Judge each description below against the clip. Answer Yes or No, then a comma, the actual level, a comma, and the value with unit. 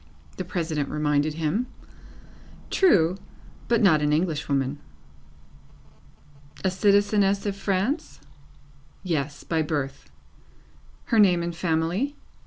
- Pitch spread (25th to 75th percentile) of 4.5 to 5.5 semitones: Yes, average, 4.8 semitones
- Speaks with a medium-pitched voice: Yes, medium, 170 Hz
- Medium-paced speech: No, slow, 100 wpm